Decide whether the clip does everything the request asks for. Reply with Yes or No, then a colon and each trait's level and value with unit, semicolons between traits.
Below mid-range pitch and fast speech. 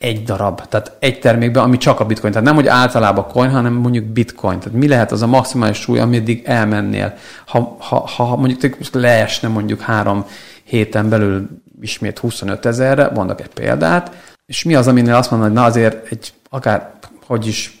Yes: low, 115 Hz; fast, 180 wpm